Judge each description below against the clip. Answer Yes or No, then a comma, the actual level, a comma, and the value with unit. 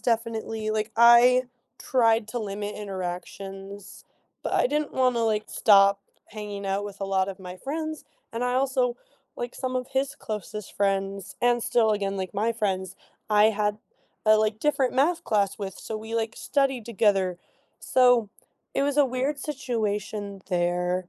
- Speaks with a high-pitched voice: Yes, high, 215 Hz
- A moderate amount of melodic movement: Yes, average, 3.8 semitones